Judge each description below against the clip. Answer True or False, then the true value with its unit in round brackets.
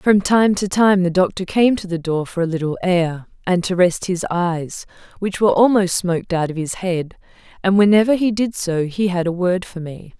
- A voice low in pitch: False (185 Hz)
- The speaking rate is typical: False (225 wpm)